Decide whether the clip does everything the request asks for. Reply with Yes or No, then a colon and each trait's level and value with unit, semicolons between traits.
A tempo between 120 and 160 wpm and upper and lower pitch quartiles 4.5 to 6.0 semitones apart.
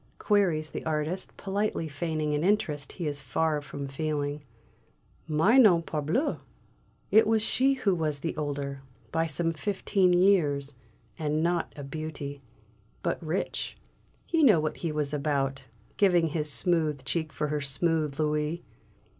No: average, 145 wpm; average, 3.3 semitones